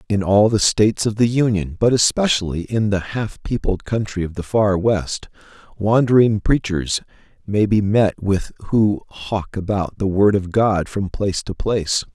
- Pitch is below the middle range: Yes, low, 100 Hz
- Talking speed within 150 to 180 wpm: Yes, average, 175 wpm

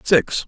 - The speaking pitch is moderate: Yes, medium, 145 Hz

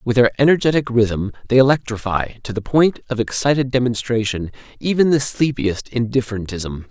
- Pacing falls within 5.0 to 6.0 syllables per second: Yes, 5.3 syllables/s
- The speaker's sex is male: Yes, male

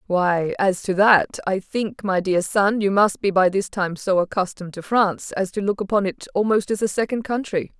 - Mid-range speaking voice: No, high, 195 Hz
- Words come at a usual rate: No, fast, 215 wpm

